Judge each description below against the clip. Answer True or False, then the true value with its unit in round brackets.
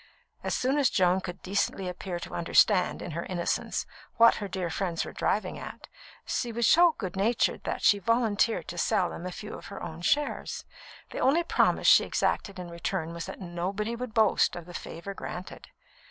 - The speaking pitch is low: False (190 Hz)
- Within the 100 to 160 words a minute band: False (195 wpm)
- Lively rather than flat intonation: False (4.3 semitones)